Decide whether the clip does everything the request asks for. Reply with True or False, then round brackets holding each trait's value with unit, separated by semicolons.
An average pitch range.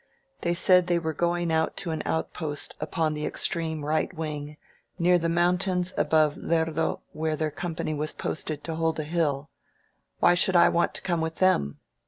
False (1.9 semitones)